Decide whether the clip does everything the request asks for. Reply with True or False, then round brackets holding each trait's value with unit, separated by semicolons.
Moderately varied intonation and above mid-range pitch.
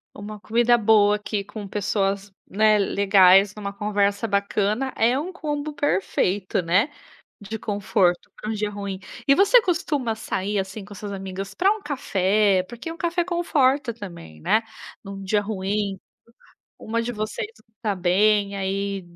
True (3.1 semitones; 205 Hz)